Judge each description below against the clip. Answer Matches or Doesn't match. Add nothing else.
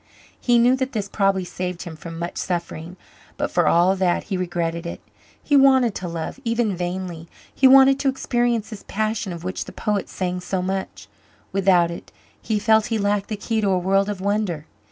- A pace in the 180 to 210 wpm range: Matches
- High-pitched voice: Matches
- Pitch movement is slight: Doesn't match